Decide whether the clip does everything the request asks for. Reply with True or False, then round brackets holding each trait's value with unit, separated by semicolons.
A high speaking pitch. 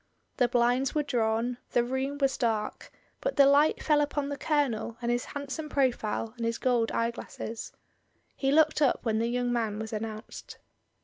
True (245 Hz)